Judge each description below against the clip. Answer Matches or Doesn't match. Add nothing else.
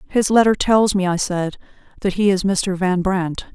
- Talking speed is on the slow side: Doesn't match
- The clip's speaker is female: Matches